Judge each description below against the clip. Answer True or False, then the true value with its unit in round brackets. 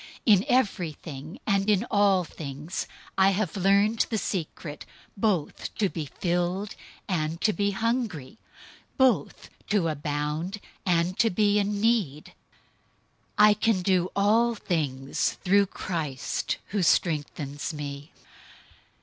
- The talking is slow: True (120 wpm)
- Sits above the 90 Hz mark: True (185 Hz)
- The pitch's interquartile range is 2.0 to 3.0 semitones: False (5.0 semitones)